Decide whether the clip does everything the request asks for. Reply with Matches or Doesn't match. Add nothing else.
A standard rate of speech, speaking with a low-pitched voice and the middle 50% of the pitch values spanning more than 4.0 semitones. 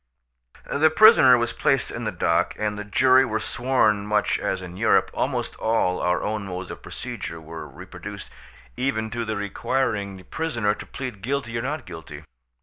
Matches